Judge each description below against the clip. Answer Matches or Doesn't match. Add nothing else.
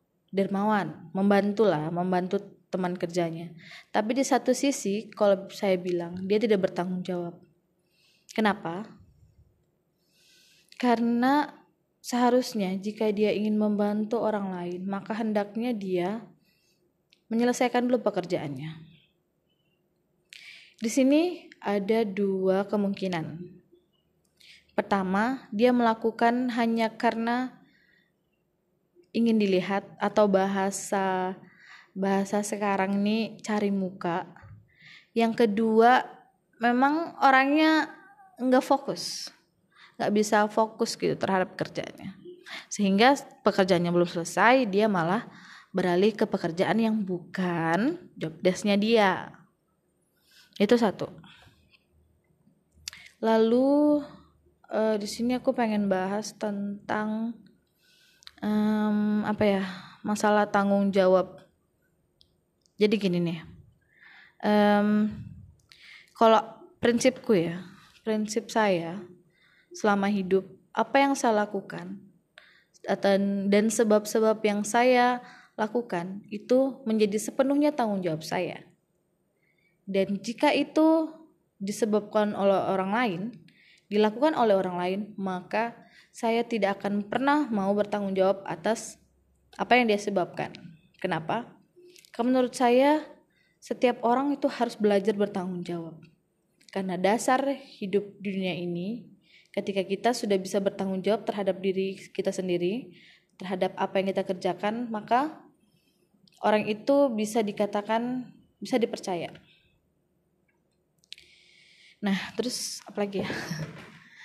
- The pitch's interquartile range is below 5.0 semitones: Matches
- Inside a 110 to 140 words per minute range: Doesn't match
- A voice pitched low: Doesn't match